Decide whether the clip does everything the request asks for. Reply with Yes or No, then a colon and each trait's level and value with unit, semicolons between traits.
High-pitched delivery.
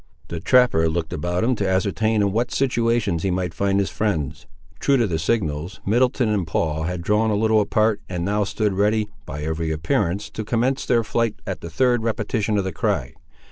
No: low, 100 Hz